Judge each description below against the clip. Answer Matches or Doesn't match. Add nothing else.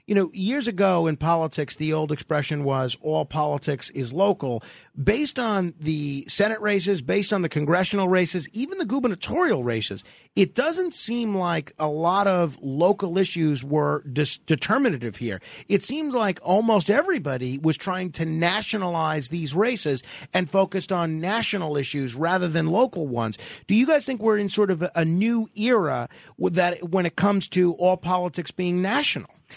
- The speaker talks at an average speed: Matches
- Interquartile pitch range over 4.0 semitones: Matches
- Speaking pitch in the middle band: Matches